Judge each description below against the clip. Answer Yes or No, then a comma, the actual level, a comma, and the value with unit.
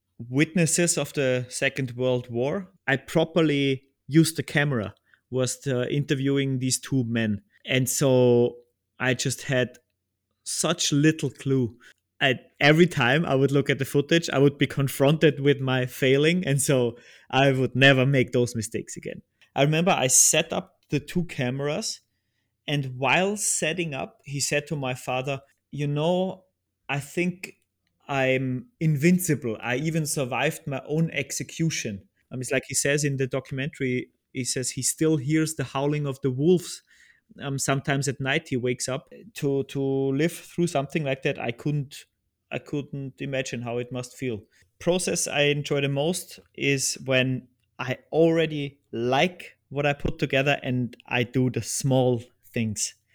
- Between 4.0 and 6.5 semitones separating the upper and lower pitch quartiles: No, average, 2.9 semitones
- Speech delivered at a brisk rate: No, average, 155 wpm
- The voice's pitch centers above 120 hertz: Yes, low, 135 Hz